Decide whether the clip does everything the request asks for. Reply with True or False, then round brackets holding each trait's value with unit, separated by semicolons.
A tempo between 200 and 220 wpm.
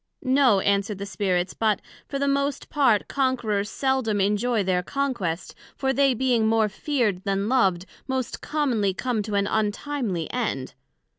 False (150 wpm)